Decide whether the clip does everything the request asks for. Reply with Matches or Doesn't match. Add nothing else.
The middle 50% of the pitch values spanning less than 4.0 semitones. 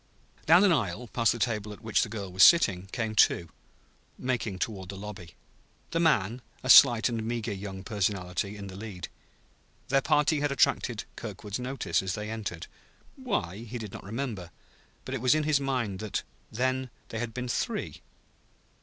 Doesn't match